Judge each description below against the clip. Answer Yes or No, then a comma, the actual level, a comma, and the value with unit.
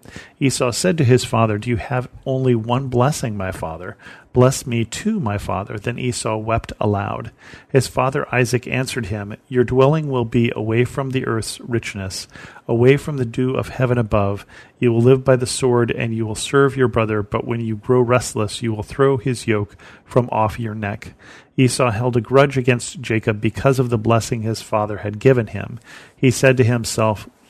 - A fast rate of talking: No, average, 190 wpm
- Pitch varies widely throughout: No, average, 2.9 semitones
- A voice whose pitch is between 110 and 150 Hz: Yes, low, 120 Hz